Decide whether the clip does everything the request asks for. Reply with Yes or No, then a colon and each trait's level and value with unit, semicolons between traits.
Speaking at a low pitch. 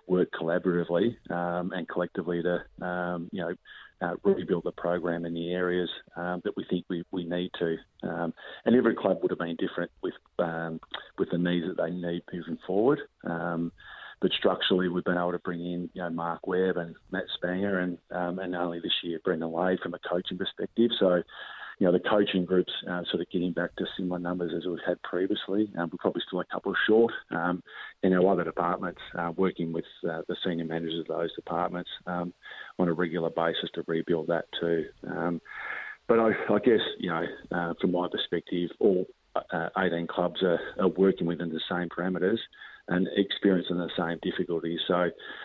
Yes: very low, 90 Hz